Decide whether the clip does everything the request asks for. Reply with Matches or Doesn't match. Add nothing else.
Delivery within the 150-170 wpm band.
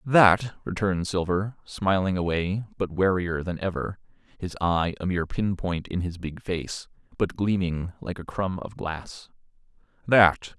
Matches